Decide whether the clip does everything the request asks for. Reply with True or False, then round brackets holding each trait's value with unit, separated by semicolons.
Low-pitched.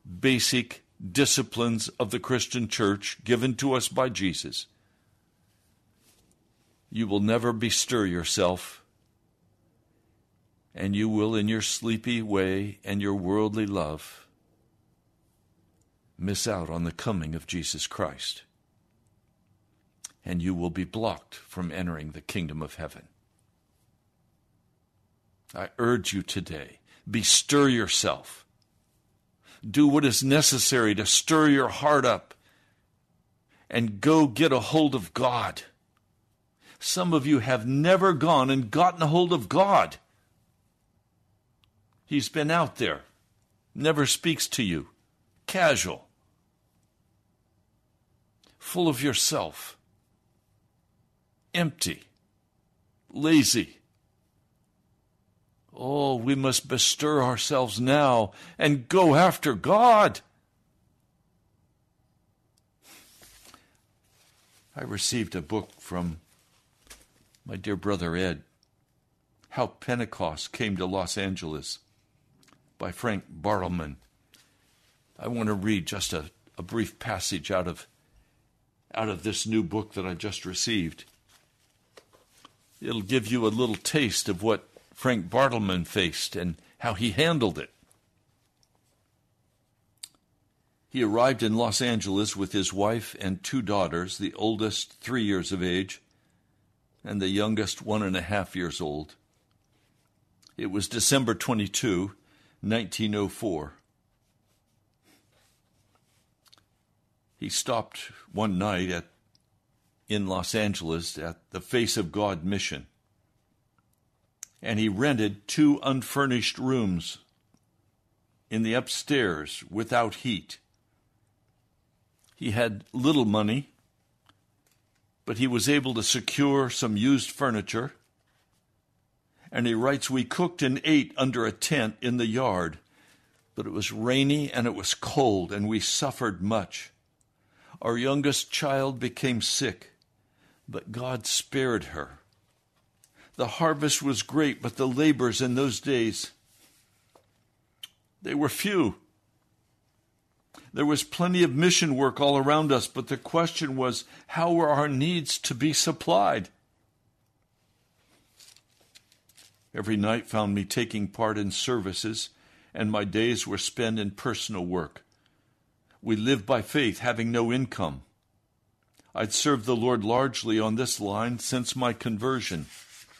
True (110 Hz)